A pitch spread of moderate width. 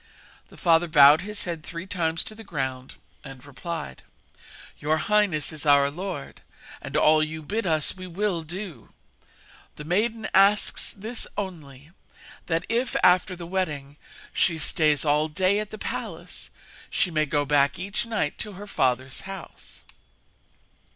Yes: average, 4.6 semitones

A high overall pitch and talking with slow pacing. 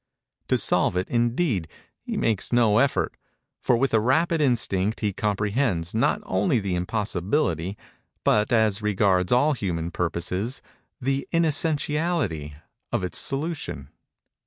No: low, 110 Hz; slow, 125 wpm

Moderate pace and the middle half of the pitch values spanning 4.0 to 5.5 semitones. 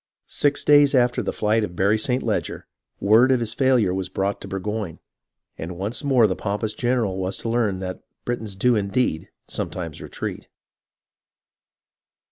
Yes: average, 150 wpm; average, 4.3 semitones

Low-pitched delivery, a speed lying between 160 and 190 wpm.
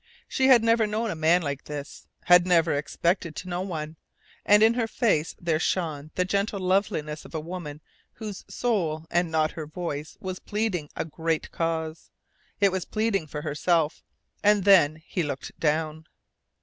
No: medium, 170 Hz; average, 175 wpm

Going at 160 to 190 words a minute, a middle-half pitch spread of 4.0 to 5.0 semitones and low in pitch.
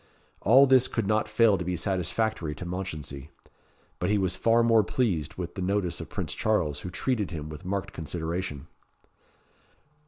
Yes: average, 165 wpm; average, 4.6 semitones; very low, 95 Hz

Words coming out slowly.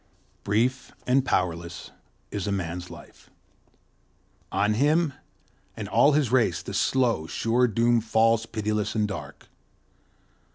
Yes: slow, 115 wpm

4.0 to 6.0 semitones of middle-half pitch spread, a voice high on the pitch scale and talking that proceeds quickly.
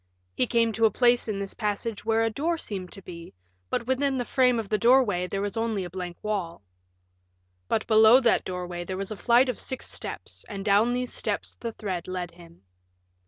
Yes: average, 4.3 semitones; high, 215 Hz; fast, 210 wpm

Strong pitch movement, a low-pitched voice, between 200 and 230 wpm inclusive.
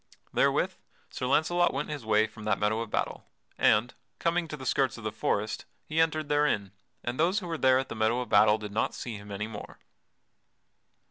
Yes: wide, 6.0 semitones; low, 120 Hz; fast, 205 wpm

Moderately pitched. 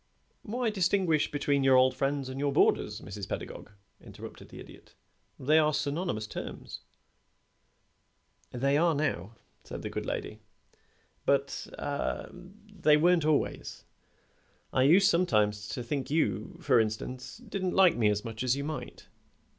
Yes: medium, 145 Hz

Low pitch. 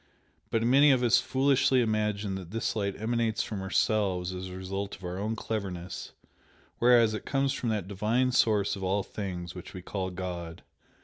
Yes: low, 105 Hz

